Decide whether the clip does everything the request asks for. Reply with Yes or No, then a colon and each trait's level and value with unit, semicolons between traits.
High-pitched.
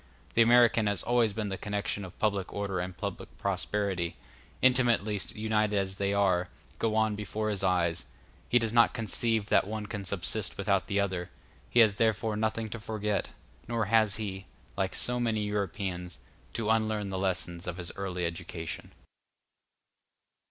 No: low, 105 Hz